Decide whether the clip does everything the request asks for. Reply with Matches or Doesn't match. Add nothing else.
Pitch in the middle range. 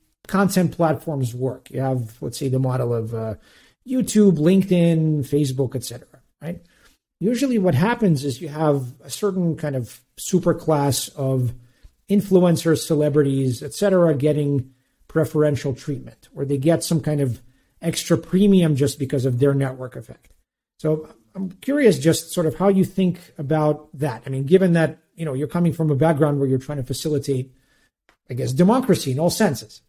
Matches